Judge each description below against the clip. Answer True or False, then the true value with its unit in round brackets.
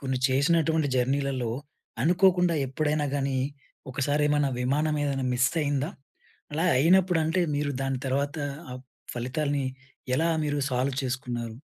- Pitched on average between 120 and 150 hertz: True (140 Hz)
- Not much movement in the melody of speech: False (3.0 semitones)